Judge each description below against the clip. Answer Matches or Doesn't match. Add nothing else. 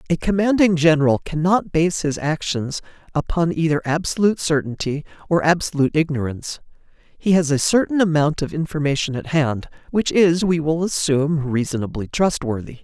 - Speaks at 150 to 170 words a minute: Doesn't match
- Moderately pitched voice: Matches